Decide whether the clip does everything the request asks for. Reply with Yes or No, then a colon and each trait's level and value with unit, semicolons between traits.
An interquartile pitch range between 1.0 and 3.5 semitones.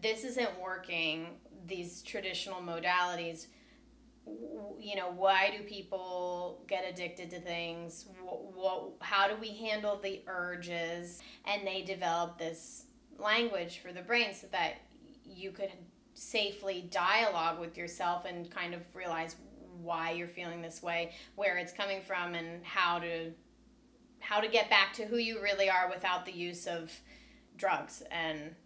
Yes: average, 3.0 semitones